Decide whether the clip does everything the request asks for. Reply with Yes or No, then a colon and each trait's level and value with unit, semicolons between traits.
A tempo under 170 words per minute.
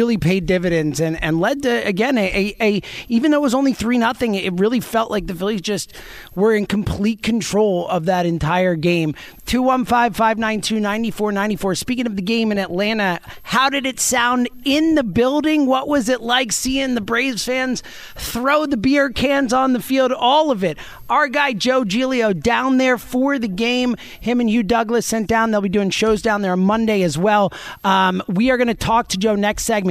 No: average, 200 wpm